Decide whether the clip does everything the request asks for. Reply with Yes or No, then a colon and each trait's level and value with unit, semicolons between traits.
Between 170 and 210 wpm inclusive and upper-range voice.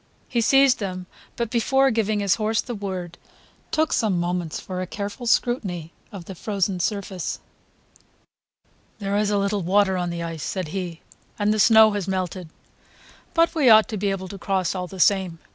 Yes: average, 180 wpm; high, 200 Hz